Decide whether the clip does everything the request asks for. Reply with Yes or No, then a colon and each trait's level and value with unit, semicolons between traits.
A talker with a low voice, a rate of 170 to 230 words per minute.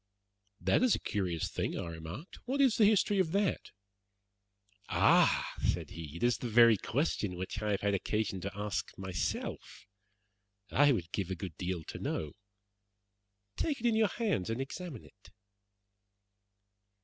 No: low, 105 Hz; average, 160 wpm